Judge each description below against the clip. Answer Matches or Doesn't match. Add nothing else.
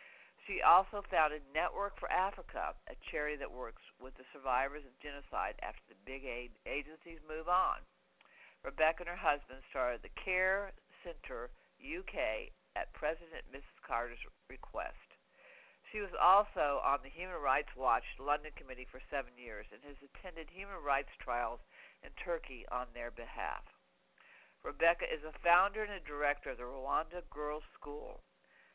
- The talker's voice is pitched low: Doesn't match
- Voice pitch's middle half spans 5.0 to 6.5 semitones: Matches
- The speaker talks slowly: Doesn't match